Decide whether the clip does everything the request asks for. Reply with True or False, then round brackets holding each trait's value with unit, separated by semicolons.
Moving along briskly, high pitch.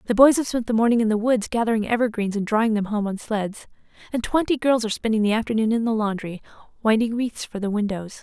True (235 wpm; 220 Hz)